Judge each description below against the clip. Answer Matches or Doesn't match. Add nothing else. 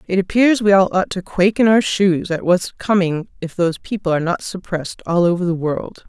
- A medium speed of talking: Doesn't match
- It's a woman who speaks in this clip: Matches